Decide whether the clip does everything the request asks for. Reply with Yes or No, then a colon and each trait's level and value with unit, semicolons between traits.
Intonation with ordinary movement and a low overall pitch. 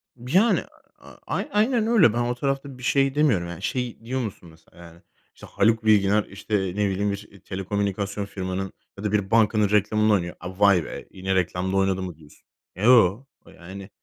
Yes: average, 3.9 semitones; low, 100 Hz